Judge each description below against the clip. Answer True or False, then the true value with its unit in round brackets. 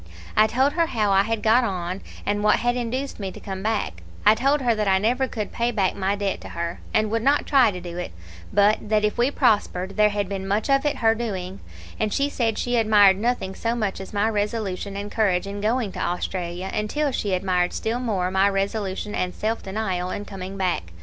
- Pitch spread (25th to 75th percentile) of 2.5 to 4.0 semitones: True (3.0 semitones)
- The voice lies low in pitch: False (210 Hz)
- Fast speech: True (225 wpm)